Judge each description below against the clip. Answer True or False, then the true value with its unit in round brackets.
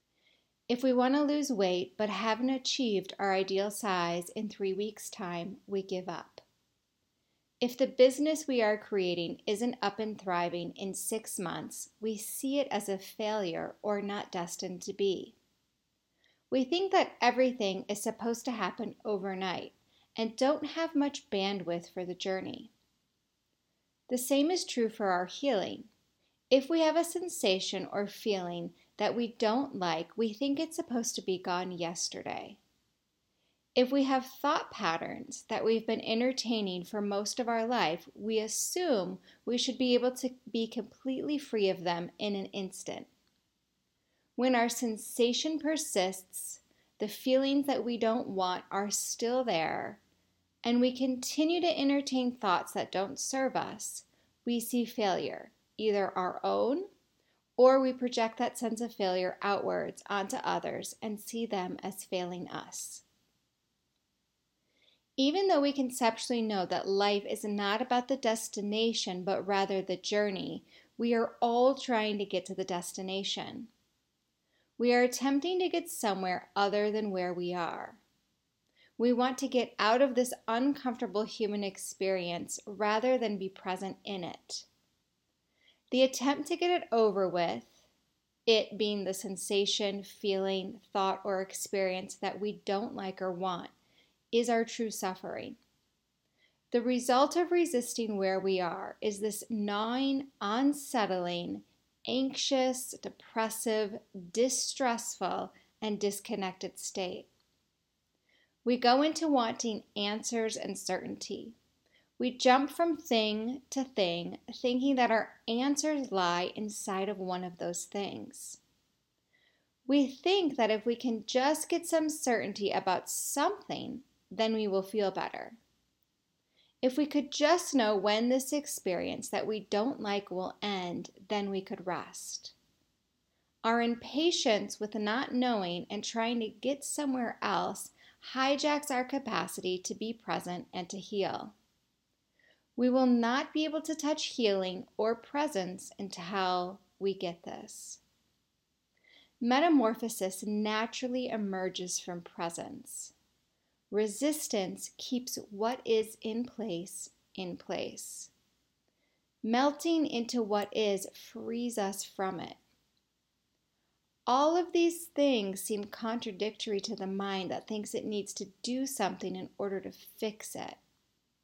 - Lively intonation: False (4.6 semitones)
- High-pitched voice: True (220 Hz)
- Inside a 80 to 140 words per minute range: True (135 wpm)